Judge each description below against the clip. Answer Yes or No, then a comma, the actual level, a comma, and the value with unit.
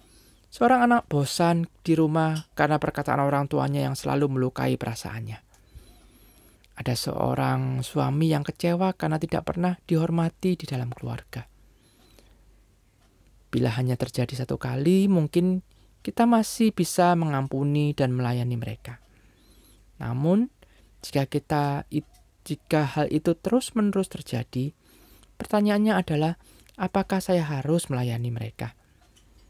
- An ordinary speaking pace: Yes, average, 110 wpm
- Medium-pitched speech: Yes, medium, 150 Hz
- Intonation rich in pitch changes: Yes, wide, 5.7 semitones